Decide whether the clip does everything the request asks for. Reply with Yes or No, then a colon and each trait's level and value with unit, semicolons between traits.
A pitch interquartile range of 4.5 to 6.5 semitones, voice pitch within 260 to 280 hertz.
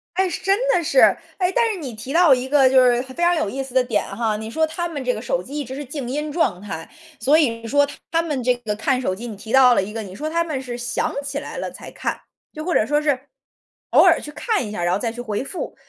Yes: average, 5.1 semitones; very high, 265 Hz